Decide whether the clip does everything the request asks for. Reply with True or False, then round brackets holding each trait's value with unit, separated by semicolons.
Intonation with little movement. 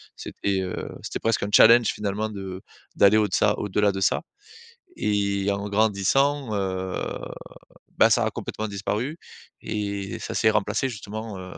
True (1.8 semitones)